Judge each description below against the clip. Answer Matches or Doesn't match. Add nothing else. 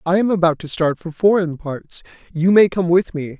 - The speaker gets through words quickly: Matches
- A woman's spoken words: Doesn't match